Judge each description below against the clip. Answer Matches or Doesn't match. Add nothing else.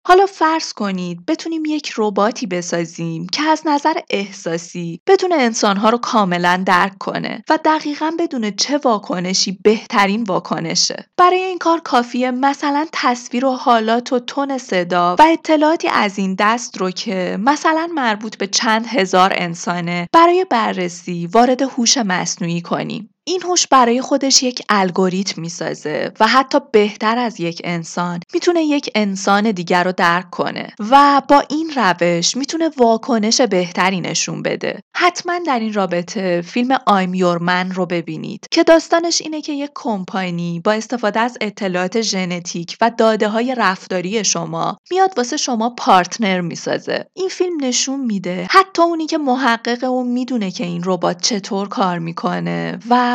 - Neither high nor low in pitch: Doesn't match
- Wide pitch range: Matches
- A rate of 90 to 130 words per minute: Doesn't match